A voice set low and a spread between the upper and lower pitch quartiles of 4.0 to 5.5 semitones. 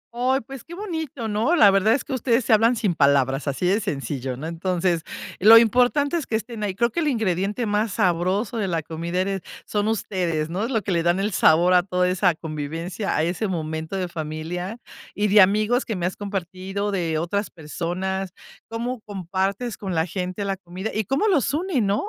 No: high, 195 Hz; average, 4.5 semitones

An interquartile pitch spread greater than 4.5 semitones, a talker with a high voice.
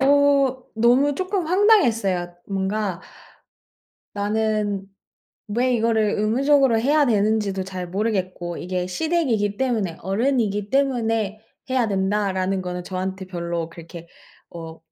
Yes: average, 5.2 semitones; high, 210 Hz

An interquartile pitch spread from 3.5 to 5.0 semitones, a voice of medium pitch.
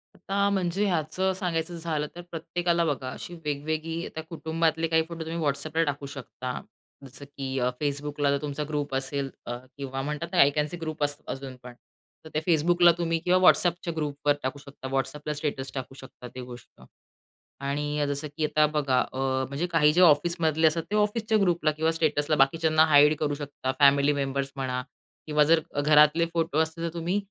No: average, 2.8 semitones; medium, 150 Hz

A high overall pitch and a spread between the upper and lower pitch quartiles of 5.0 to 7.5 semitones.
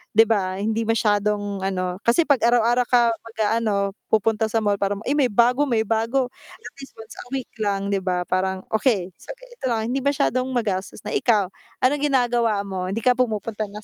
No: high, 220 Hz; average, 3.3 semitones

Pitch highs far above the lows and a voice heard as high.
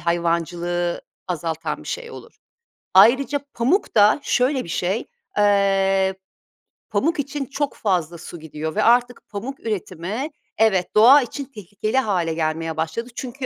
Yes: wide, 6.6 semitones; high, 205 Hz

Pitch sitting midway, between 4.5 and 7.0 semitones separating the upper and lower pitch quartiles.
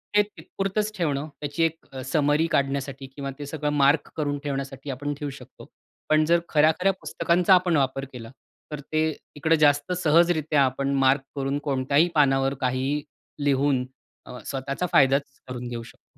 No: medium, 145 Hz; narrow, 2.5 semitones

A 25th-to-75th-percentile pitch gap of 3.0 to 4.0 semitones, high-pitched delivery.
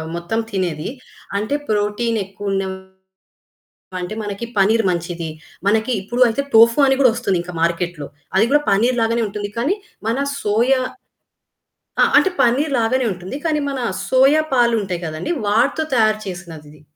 No: average, 4.8 semitones; high, 215 Hz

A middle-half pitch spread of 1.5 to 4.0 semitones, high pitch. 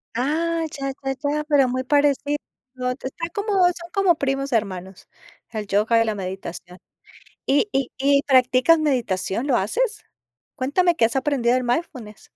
No: average, 4.6 semitones; very high, 265 Hz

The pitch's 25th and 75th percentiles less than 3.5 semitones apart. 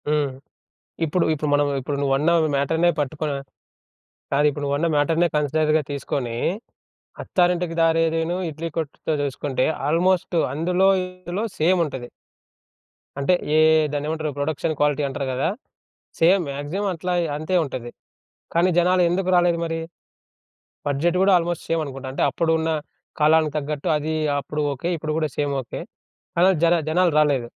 Yes: average, 3.0 semitones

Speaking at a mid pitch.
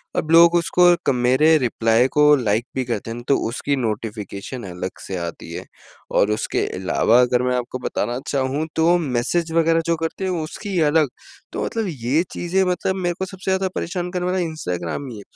Yes: medium, 145 Hz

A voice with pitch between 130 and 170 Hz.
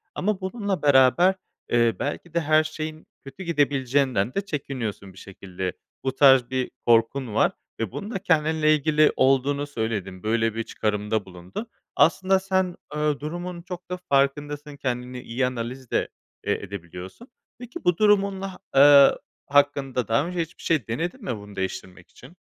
Yes: medium, 140 Hz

